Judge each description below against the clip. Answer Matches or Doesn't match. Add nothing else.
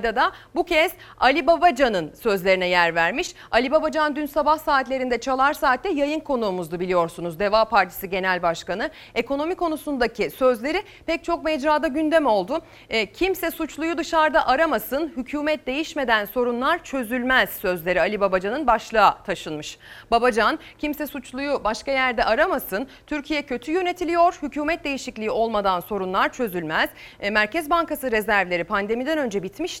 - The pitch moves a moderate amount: Doesn't match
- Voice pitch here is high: Matches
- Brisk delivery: Doesn't match